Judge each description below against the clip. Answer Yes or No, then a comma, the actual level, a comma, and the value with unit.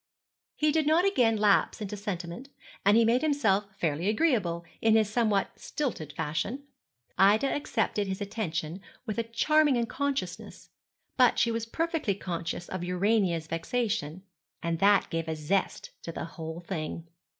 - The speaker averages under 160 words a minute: Yes, average, 150 wpm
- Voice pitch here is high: Yes, high, 205 Hz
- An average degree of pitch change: No, wide, 5.8 semitones